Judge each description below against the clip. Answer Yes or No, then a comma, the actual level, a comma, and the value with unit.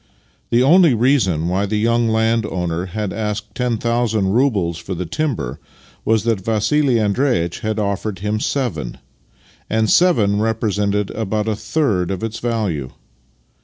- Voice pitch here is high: No, low, 110 Hz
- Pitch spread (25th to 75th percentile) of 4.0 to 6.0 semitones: No, average, 3.2 semitones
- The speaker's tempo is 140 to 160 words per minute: Yes, average, 145 wpm